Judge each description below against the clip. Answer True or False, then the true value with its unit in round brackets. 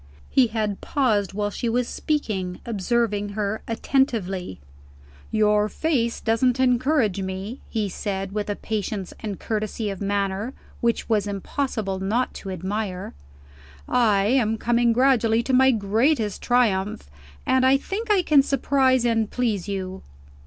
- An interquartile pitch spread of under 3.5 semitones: False (3.8 semitones)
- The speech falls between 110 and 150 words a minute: True (140 wpm)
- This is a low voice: False (220 Hz)